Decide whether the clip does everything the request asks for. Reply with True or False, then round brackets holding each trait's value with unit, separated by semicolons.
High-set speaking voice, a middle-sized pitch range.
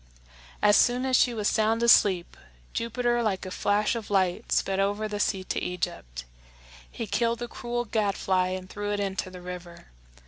True (205 Hz; 3.7 semitones)